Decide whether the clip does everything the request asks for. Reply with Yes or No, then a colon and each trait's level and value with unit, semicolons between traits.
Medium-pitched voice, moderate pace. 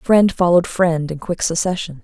Yes: medium, 175 Hz; average, 175 wpm